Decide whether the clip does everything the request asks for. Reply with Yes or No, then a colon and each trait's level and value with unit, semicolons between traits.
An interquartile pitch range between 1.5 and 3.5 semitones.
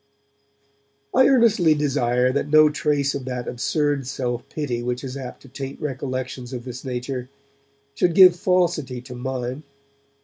Yes: average, 3.2 semitones